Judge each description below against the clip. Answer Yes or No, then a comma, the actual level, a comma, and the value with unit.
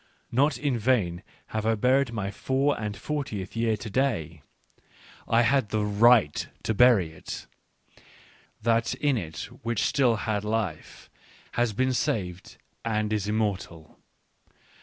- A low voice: Yes, low, 110 Hz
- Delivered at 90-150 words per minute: Yes, average, 140 wpm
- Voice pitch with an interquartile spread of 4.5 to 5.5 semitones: No, average, 3.6 semitones